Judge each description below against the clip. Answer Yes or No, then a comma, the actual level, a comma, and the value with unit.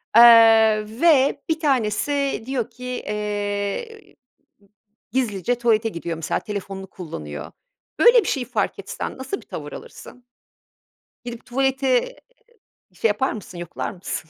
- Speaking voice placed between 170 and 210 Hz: No, high, 230 Hz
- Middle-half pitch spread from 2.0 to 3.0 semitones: No, average, 4.5 semitones